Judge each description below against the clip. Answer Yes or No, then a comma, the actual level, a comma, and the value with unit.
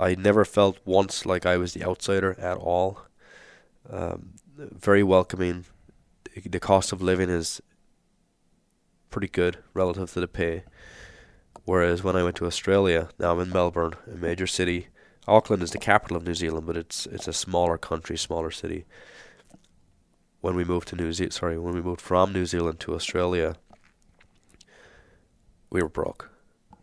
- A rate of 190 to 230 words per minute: No, average, 160 wpm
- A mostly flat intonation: Yes, narrow, 1.5 semitones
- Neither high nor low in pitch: No, very low, 90 Hz